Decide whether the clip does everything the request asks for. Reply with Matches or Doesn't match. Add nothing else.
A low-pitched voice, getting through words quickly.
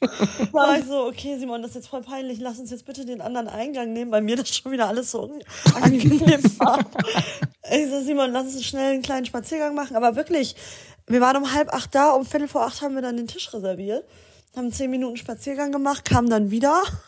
Doesn't match